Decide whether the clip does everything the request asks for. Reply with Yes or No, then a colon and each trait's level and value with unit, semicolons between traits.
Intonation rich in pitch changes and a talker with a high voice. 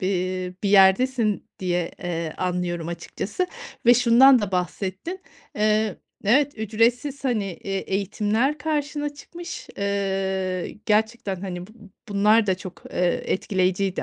No: average, 4.2 semitones; high, 200 Hz